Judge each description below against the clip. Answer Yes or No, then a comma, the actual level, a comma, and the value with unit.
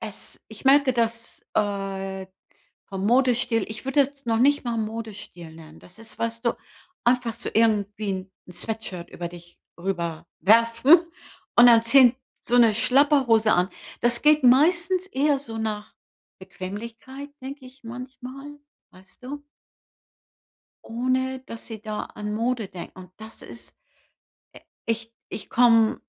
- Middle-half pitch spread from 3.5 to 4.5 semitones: Yes, average, 3.9 semitones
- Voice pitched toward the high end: Yes, high, 230 Hz